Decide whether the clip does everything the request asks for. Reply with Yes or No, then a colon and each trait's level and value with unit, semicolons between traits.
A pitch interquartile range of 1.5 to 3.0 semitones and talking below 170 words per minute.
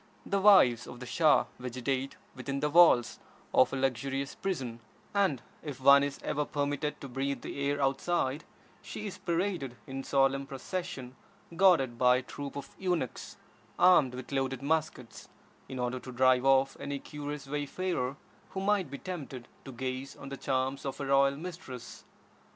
Yes: narrow, 2.4 semitones; average, 160 wpm